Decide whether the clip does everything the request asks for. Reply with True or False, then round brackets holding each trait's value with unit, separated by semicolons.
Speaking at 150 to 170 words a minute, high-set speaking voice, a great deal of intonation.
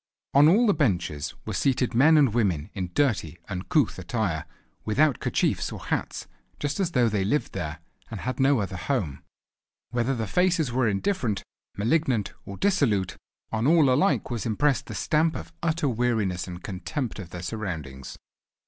False (165 wpm; 120 Hz; 7.2 semitones)